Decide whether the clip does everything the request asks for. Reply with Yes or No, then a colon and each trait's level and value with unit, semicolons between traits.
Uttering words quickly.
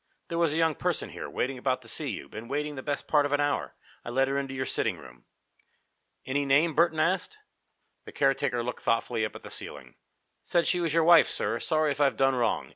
Yes: fast, 230 wpm